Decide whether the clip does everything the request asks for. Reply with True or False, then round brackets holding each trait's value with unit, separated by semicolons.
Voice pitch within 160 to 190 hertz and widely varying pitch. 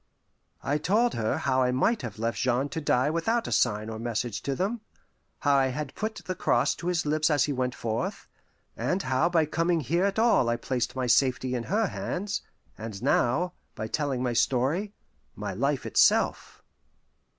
False (140 Hz; 6.2 semitones)